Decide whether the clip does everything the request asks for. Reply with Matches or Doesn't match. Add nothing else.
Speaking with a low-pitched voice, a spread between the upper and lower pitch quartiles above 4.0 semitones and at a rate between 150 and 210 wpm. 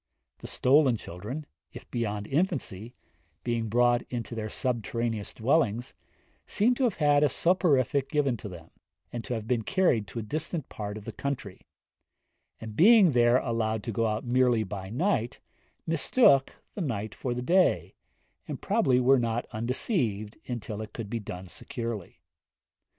Matches